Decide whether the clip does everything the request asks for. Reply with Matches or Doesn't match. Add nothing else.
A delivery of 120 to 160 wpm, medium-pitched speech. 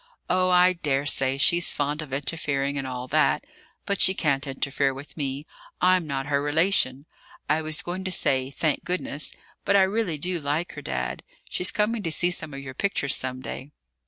Doesn't match